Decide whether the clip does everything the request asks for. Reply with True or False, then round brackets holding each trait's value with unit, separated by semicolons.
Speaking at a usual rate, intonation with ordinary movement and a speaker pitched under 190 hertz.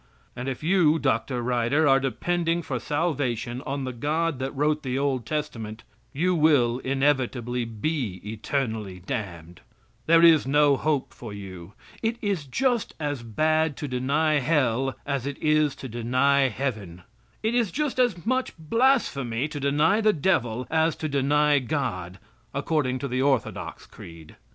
True (150 wpm; 4.4 semitones; 140 Hz)